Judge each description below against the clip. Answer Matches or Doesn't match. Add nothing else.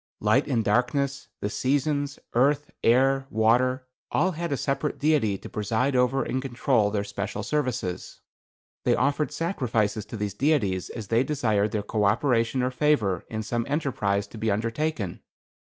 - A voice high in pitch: Doesn't match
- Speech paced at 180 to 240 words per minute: Doesn't match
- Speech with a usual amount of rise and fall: Matches